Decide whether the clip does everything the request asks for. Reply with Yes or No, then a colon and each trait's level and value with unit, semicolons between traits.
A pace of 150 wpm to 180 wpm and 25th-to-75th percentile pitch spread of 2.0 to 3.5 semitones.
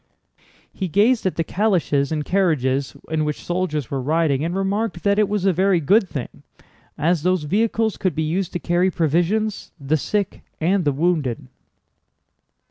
No: average, 165 wpm; average, 4.5 semitones